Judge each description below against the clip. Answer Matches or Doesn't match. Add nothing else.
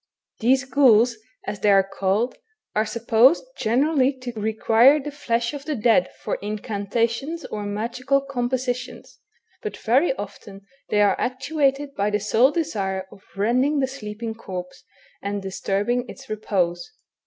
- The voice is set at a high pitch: Matches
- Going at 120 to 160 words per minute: Matches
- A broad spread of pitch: Doesn't match